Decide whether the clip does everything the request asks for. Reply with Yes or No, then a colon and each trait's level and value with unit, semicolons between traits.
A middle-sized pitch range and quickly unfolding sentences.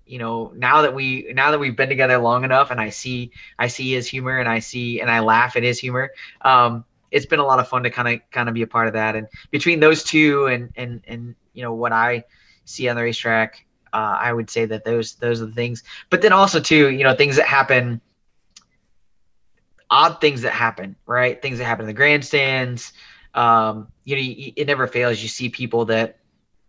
No: narrow, 2.3 semitones; fast, 225 wpm